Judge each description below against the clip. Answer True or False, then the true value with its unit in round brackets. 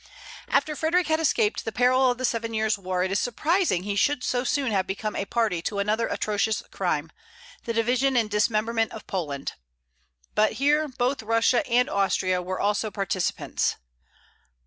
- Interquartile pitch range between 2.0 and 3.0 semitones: False (4.1 semitones)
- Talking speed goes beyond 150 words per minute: True (170 wpm)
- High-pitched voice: True (225 Hz)